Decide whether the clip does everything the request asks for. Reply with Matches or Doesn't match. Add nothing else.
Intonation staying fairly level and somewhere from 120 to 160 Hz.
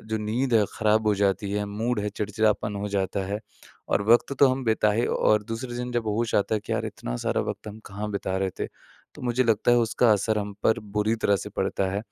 Doesn't match